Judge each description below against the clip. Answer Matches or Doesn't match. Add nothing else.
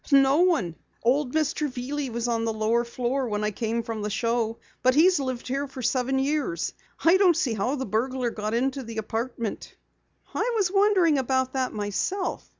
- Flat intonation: Doesn't match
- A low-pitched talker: Doesn't match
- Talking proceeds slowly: Doesn't match